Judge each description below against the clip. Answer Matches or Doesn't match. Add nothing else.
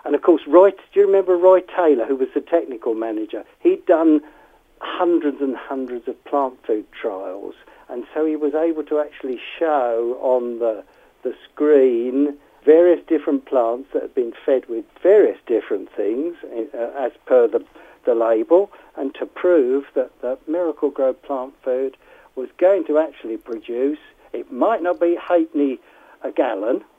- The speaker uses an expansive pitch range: Matches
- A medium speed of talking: Matches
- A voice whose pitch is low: Doesn't match